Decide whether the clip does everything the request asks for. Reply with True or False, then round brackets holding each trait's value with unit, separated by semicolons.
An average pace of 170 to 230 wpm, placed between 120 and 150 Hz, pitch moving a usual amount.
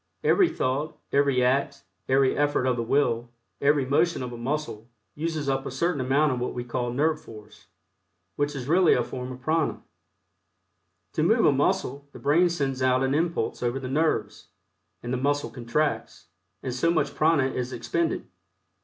True (175 wpm; 135 Hz; 3.2 semitones)